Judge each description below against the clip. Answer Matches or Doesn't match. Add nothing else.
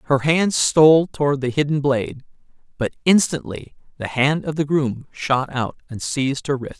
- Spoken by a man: Matches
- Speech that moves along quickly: Doesn't match